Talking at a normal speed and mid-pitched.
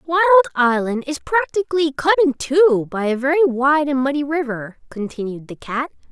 No: average, 165 wpm; very high, 285 Hz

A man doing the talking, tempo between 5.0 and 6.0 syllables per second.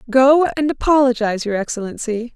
No: female; 5.7 syllables/s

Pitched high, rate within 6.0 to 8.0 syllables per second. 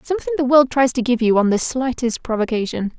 Yes: very high, 250 Hz; 6.2 syllables/s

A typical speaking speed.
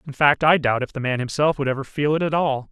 No: fast, 310 wpm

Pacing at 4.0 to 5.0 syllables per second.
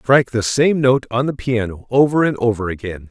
No: 5.4 syllables/s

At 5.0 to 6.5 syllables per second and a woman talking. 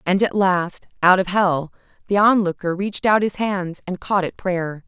No: 4.5 syllables/s; female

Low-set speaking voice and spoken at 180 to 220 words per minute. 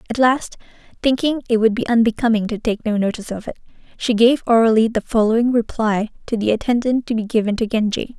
No: high, 225 Hz; average, 200 wpm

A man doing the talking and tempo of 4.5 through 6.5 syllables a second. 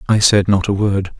Yes: male; 4.9 syllables/s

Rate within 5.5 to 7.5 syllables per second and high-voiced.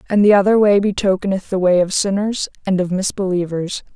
Yes: 5.7 syllables/s; high, 195 Hz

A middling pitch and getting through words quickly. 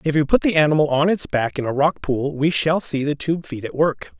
Yes: medium, 150 Hz; fast, 285 wpm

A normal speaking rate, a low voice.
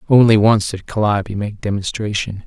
Yes: average, 145 wpm; low, 105 Hz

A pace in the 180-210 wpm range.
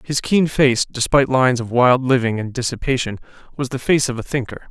Yes: fast, 205 wpm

